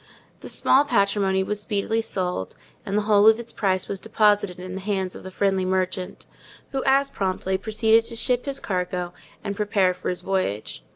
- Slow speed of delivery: No, average, 185 wpm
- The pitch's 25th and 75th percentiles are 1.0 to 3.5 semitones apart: Yes, average, 2.8 semitones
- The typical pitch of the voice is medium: No, high, 200 Hz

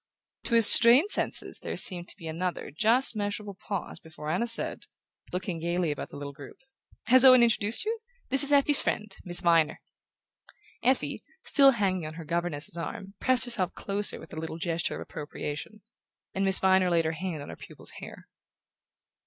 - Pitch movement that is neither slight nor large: No, wide, 5.9 semitones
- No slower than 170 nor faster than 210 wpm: Yes, average, 180 wpm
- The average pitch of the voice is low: No, high, 190 Hz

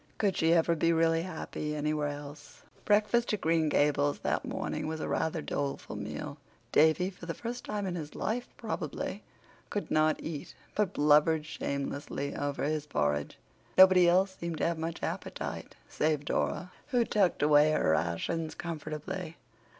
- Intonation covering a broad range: No, average, 3.3 semitones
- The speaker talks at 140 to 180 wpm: Yes, average, 160 wpm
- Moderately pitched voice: Yes, medium, 160 Hz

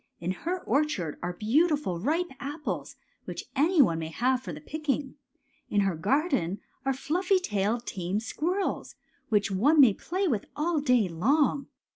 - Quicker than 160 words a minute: No, average, 155 wpm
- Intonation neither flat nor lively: No, wide, 7.9 semitones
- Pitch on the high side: Yes, very high, 265 Hz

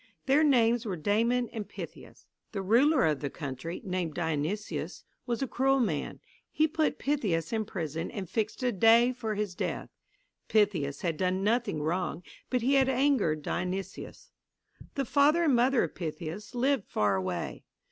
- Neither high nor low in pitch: No, high, 210 Hz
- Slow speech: No, average, 160 wpm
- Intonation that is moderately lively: No, wide, 7.0 semitones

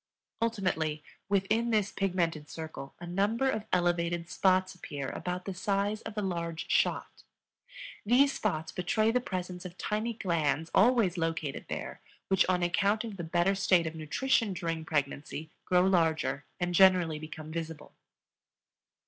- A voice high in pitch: No, medium, 180 Hz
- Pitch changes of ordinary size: Yes, average, 3.7 semitones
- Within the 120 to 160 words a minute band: Yes, average, 145 wpm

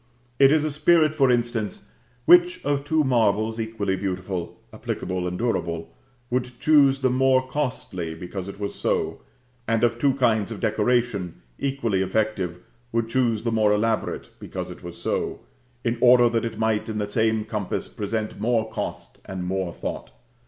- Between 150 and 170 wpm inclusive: Yes, average, 165 wpm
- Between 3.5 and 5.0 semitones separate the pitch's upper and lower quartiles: Yes, average, 3.9 semitones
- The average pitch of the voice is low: Yes, low, 115 Hz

